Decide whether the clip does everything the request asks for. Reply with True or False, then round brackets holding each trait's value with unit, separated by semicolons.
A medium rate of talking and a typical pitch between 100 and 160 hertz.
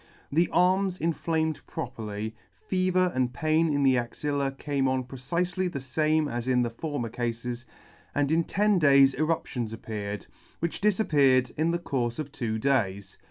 True (160 wpm; 140 Hz)